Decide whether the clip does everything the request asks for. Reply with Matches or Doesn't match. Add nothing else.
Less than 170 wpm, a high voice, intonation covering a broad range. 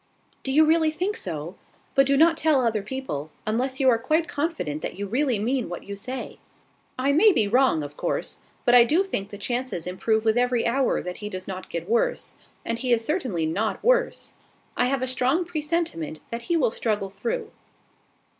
Doesn't match